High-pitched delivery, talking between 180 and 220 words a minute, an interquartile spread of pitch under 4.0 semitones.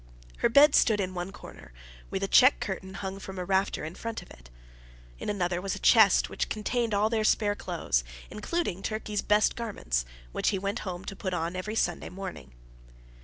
Yes: high, 195 Hz; average, 195 wpm; average, 2.9 semitones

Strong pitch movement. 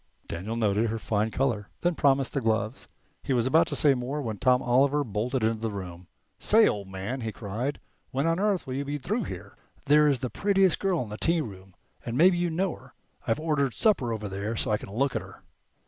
Yes: wide, 5.7 semitones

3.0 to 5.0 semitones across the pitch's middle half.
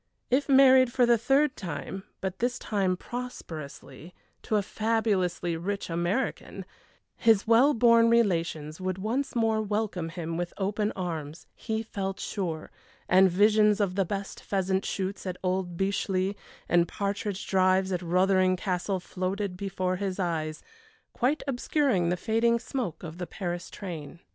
Yes: average, 3.7 semitones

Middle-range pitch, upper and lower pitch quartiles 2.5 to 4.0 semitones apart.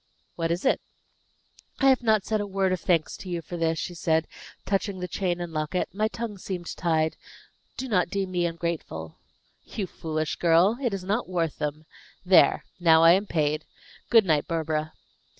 Yes: medium, 175 Hz; average, 3.4 semitones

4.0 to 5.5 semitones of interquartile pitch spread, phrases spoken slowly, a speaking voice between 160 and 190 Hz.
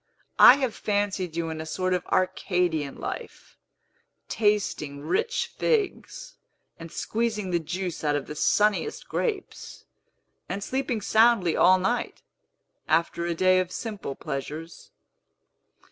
Yes: average, 5.1 semitones; slow, 125 wpm; medium, 185 Hz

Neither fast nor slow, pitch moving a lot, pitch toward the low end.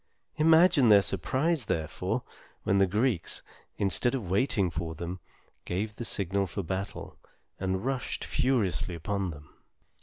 No: slow, 130 wpm; wide, 5.7 semitones; low, 100 Hz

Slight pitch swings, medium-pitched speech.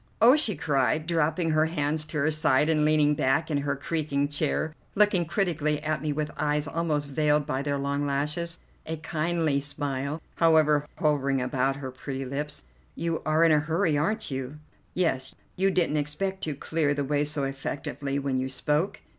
Yes: narrow, 2.3 semitones; medium, 150 Hz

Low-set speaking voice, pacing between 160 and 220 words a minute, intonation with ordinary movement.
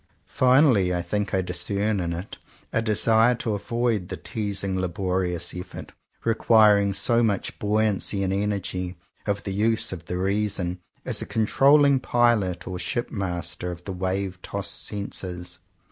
No: low, 100 Hz; average, 150 wpm; average, 3.2 semitones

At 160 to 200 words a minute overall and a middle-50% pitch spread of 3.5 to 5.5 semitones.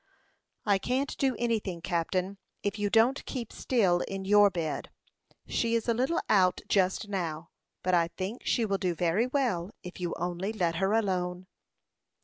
Yes: average, 165 wpm; average, 4.1 semitones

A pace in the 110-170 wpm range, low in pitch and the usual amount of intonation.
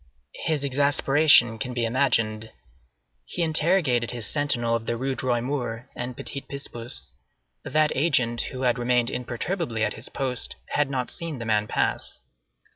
Yes: average, 150 wpm; low, 125 Hz; average, 3.3 semitones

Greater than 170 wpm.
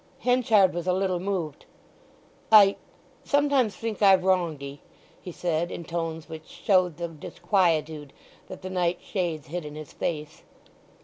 No: average, 140 wpm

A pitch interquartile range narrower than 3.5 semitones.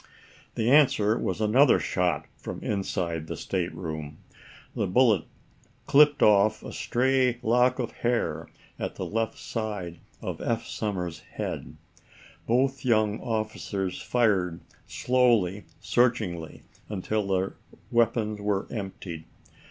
No: average, 4.3 semitones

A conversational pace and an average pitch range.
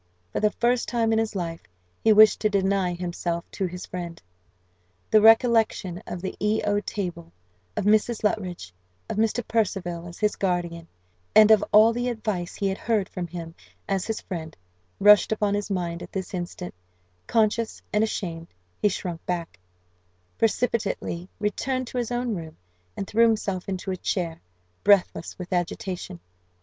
Yes: average, 160 wpm; average, 3.7 semitones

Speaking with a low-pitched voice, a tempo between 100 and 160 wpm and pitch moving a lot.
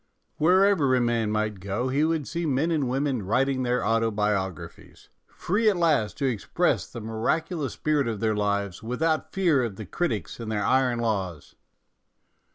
No: low, 125 Hz; average, 170 wpm; wide, 6.1 semitones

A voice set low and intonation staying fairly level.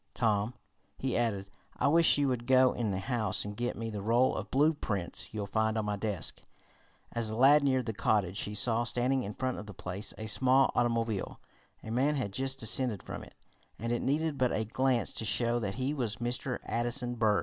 No: low, 120 Hz; average, 3.4 semitones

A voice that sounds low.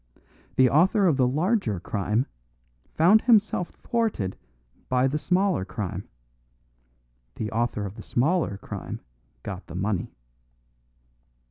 Yes: low, 130 Hz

